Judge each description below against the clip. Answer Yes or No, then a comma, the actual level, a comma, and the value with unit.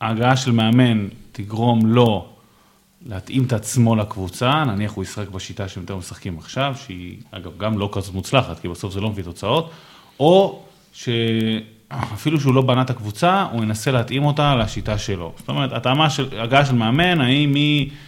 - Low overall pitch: Yes, low, 115 Hz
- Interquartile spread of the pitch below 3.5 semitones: No, average, 4.8 semitones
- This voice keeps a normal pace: No, fast, 165 wpm